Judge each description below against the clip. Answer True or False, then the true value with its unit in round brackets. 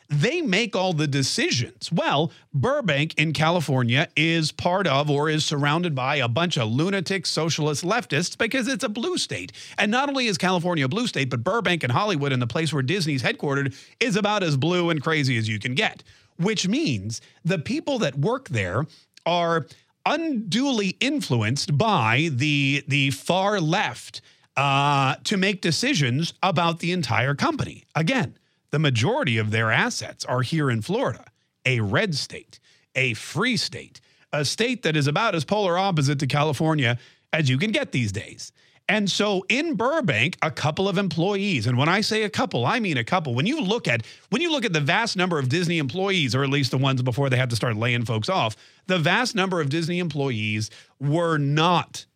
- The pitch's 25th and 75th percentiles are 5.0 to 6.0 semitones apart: True (5.5 semitones)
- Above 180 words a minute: True (190 wpm)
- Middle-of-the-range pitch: True (155 Hz)